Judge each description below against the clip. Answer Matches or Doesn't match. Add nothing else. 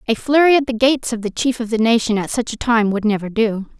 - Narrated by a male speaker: Doesn't match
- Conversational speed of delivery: Doesn't match